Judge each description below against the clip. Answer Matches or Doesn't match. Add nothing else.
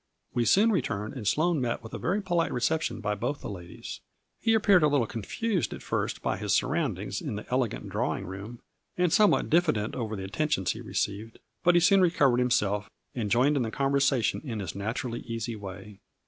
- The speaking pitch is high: Doesn't match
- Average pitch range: Doesn't match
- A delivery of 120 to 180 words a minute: Doesn't match